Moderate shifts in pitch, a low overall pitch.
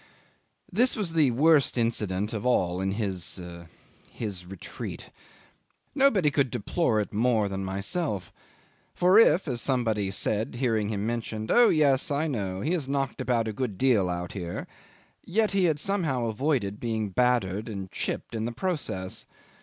No: wide, 6.6 semitones; low, 115 Hz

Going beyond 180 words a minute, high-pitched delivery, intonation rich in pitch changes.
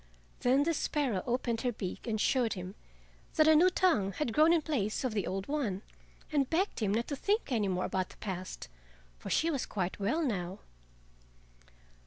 Yes: average, 190 wpm; high, 240 Hz; wide, 7.5 semitones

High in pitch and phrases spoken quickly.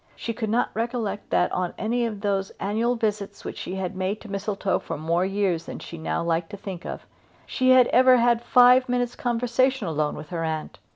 Yes: high, 205 Hz; fast, 210 wpm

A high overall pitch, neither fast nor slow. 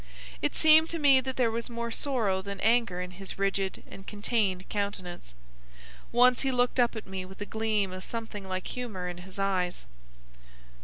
Yes: high, 205 Hz; average, 185 wpm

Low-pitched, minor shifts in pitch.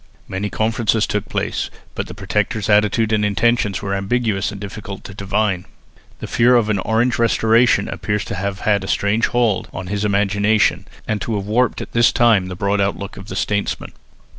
Yes: low, 105 Hz; narrow, 2.1 semitones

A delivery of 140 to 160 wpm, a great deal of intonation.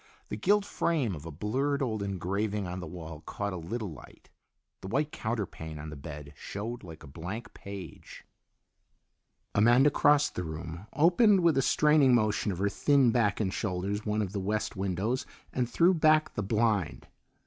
No: average, 175 wpm; wide, 6.1 semitones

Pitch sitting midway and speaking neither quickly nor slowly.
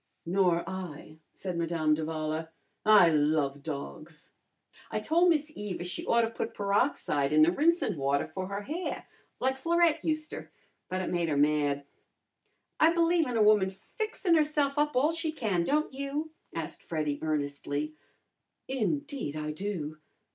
No: high, 195 Hz; average, 150 wpm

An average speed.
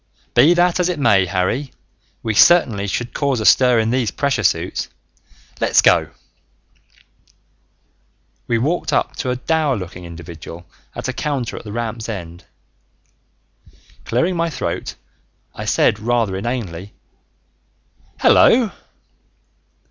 No: slow, 125 wpm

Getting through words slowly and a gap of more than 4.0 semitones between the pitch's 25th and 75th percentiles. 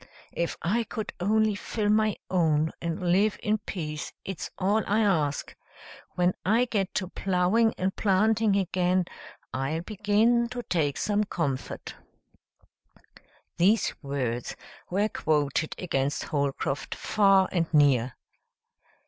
Yes: slow, 120 wpm; average, 5.2 semitones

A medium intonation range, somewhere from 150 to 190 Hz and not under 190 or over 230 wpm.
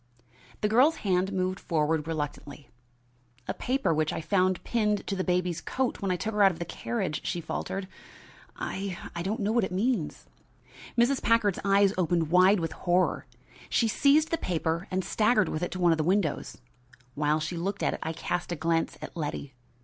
Yes: average, 4.0 semitones; medium, 185 Hz; average, 195 wpm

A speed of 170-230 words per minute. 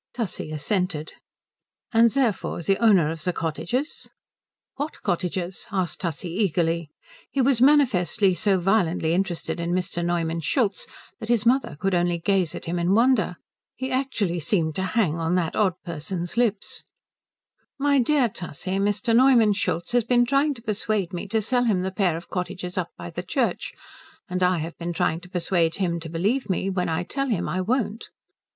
Yes: average, 175 wpm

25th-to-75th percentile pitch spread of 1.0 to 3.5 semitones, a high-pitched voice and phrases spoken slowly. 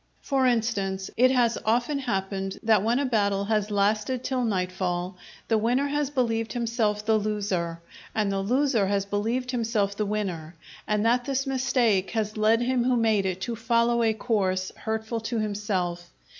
No: average, 3.2 semitones; high, 220 Hz; average, 170 wpm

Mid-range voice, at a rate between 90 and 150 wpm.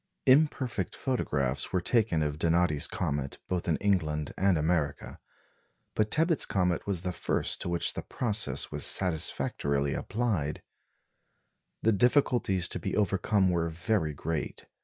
No: very low, 90 Hz; slow, 135 wpm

